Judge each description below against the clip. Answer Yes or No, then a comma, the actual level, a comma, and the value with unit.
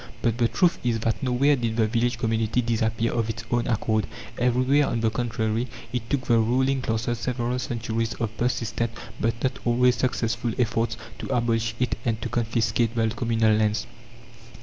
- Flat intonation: Yes, narrow, 1.6 semitones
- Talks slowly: No, average, 170 wpm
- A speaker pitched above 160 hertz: No, low, 115 Hz